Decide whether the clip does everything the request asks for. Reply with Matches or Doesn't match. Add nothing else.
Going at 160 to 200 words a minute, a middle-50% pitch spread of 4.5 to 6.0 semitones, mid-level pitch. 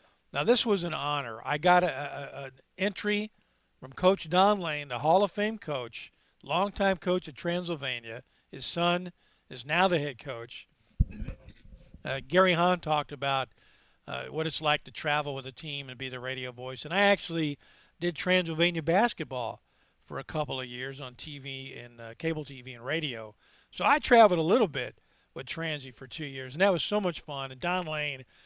Matches